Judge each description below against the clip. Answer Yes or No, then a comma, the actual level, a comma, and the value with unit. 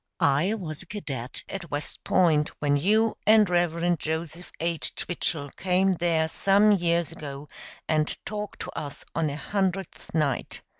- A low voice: No, medium, 170 Hz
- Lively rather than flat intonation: No, average, 3.9 semitones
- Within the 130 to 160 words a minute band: Yes, average, 150 wpm